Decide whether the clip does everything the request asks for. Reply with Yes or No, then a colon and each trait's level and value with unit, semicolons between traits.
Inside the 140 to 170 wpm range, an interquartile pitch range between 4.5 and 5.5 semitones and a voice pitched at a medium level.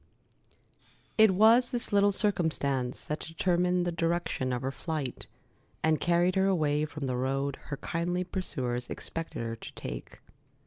Yes: average, 145 wpm; average, 5.0 semitones; medium, 165 Hz